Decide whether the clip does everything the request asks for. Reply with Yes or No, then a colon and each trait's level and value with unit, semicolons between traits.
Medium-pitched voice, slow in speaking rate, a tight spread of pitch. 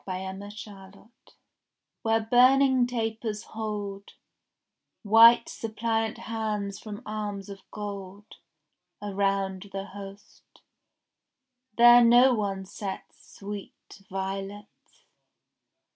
No: high, 205 Hz; slow, 85 wpm; narrow, 2.2 semitones